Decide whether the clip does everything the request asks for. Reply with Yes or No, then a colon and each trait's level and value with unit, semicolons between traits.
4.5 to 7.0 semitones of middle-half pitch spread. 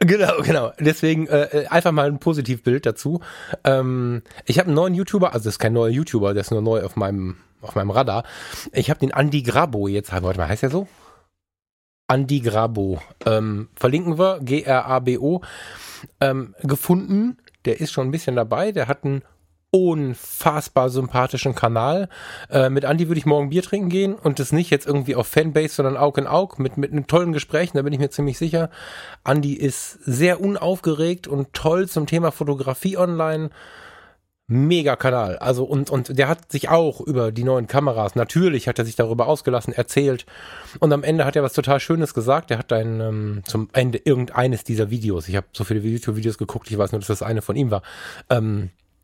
Yes: average, 5.2 semitones